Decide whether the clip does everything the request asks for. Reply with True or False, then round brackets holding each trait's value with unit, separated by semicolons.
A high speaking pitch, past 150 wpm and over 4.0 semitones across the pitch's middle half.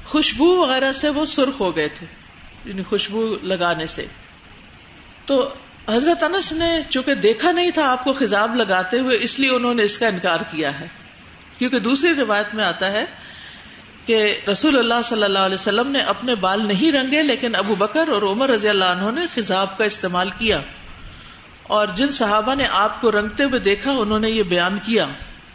True (220 Hz; 185 wpm; 5.3 semitones)